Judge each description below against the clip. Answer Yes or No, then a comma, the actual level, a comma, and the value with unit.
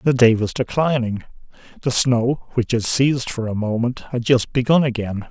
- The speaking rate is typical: Yes, average, 180 wpm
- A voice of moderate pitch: No, low, 120 Hz